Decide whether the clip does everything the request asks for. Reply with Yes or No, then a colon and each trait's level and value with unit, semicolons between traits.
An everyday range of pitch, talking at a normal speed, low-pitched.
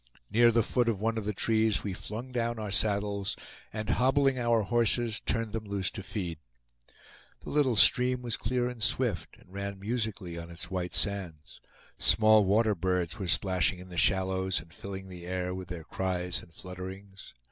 Yes: average, 3.7 semitones; average, 180 wpm; low, 100 Hz